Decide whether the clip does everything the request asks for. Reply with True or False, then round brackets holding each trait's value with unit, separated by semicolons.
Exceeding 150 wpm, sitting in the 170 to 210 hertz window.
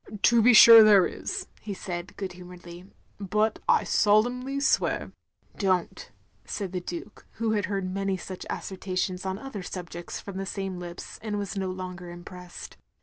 True (190 wpm; 190 Hz)